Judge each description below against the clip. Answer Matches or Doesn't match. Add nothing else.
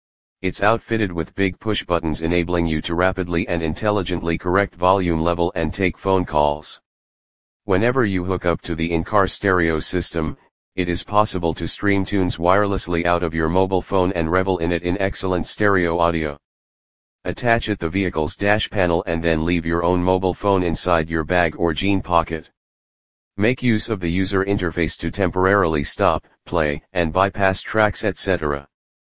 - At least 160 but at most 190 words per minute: Matches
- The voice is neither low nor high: Doesn't match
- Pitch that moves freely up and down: Doesn't match